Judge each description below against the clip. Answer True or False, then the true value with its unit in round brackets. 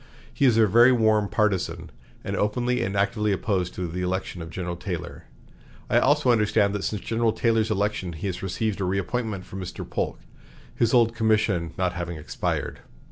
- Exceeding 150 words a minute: True (180 wpm)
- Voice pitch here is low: True (105 Hz)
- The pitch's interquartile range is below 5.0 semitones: True (3.5 semitones)